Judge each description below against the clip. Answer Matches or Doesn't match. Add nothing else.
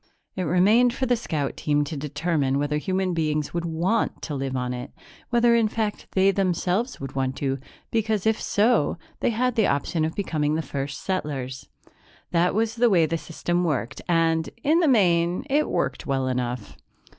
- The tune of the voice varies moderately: Doesn't match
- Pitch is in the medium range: Matches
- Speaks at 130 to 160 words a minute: Doesn't match